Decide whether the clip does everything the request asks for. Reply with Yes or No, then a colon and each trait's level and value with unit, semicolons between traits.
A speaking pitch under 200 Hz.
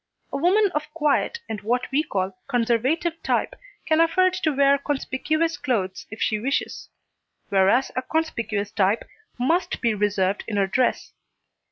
No: very high, 260 Hz